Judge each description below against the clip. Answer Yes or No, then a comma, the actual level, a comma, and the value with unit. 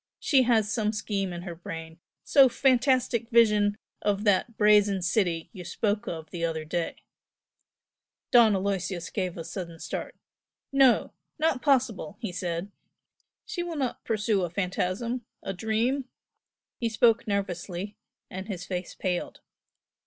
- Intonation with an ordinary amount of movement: Yes, average, 4.7 semitones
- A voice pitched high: Yes, high, 205 Hz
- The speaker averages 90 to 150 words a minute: Yes, average, 140 wpm